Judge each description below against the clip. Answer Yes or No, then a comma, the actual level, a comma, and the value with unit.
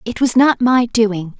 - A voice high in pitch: Yes, high, 230 Hz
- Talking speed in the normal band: No, fast, 215 wpm